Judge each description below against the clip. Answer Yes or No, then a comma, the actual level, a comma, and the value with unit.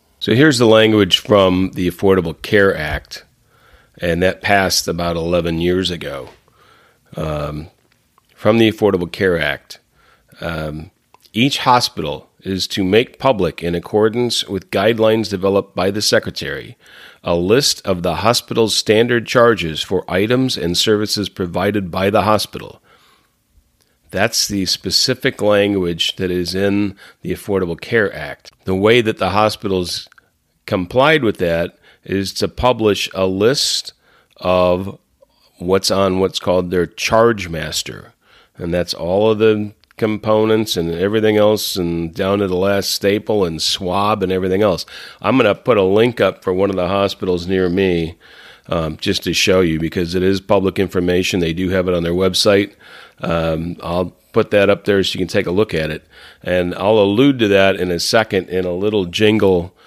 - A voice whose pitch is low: Yes, very low, 95 Hz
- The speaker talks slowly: No, average, 160 wpm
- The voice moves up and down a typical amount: Yes, average, 3.1 semitones